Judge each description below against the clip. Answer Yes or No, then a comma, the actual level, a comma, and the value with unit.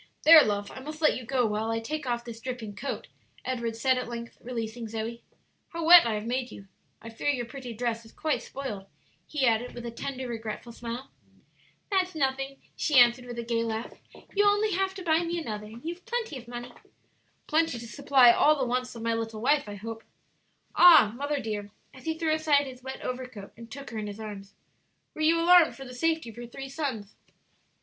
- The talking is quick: Yes, fast, 215 wpm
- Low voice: No, very high, 250 Hz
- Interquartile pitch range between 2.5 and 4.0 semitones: No, average, 4.5 semitones